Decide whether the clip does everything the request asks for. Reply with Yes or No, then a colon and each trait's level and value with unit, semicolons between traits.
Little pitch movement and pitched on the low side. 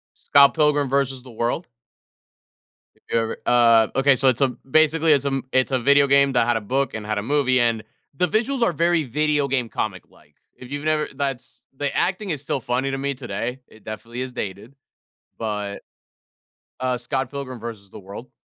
No: average, 3.3 semitones; low, 130 Hz